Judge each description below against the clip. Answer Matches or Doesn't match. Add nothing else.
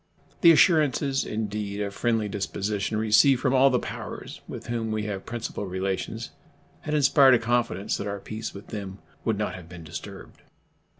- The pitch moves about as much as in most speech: Matches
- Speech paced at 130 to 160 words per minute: Doesn't match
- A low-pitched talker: Matches